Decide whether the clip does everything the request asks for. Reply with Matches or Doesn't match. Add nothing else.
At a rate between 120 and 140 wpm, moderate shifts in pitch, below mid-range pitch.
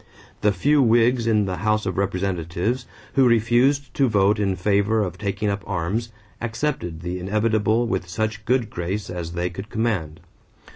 Doesn't match